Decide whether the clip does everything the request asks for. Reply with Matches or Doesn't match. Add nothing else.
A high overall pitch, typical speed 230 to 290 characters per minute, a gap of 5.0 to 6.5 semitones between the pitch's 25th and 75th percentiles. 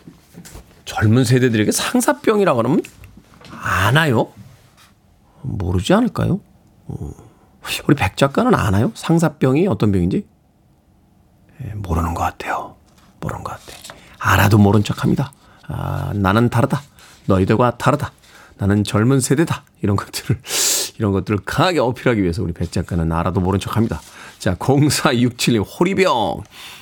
Doesn't match